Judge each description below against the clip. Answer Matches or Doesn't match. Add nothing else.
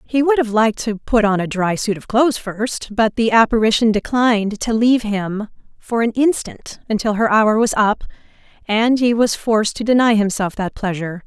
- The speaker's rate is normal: Matches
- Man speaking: Doesn't match